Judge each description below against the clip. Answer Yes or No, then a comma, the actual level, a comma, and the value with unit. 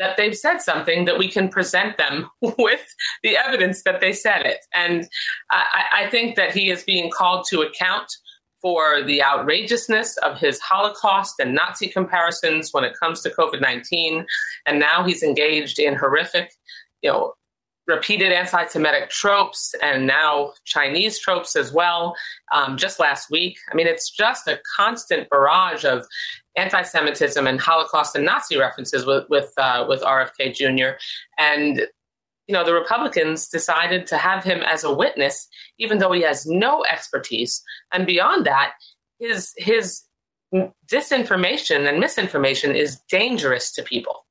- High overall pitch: No, medium, 175 Hz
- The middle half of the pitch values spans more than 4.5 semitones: Yes, average, 5.0 semitones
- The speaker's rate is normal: Yes, average, 155 wpm